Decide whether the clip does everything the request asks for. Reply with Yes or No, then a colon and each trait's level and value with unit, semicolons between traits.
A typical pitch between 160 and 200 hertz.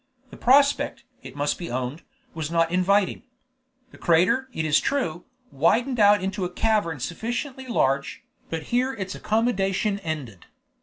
Yes: medium, 185 Hz